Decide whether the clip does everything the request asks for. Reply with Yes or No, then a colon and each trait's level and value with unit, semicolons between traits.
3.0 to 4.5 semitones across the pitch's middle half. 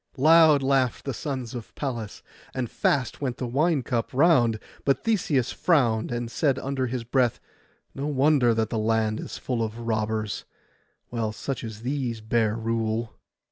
Yes: average, 3.4 semitones